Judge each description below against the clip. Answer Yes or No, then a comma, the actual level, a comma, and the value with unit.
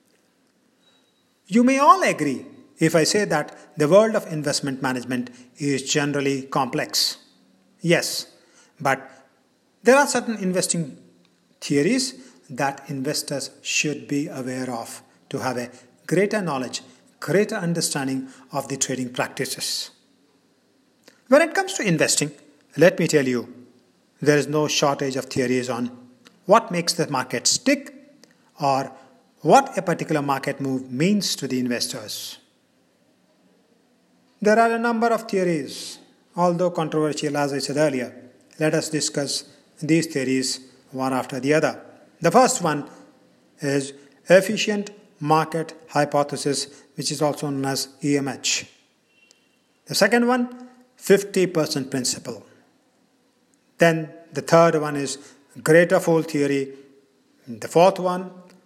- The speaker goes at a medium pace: No, slow, 125 wpm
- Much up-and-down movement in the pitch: Yes, wide, 5.9 semitones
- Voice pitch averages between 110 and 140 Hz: No, medium, 150 Hz